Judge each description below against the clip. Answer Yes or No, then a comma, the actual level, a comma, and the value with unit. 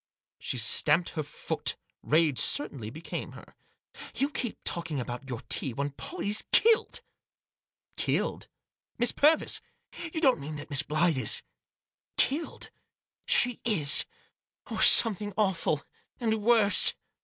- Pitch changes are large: Yes, wide, 8.6 semitones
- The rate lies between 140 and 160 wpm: Yes, average, 145 wpm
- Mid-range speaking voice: Yes, medium, 170 Hz